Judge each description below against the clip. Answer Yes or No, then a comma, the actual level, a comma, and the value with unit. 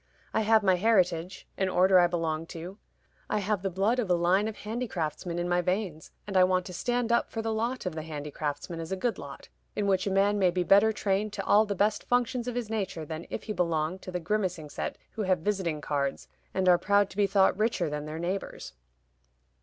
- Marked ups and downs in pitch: No, average, 3.5 semitones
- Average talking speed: No, fast, 230 wpm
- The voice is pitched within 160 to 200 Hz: Yes, high, 190 Hz